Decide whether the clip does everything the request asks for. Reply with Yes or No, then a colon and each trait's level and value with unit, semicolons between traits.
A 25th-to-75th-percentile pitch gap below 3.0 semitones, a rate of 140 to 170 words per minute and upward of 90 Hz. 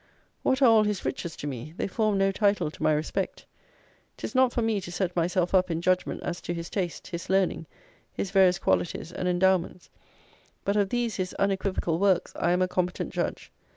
No: narrow, 2.4 semitones; average, 200 wpm; medium, 185 Hz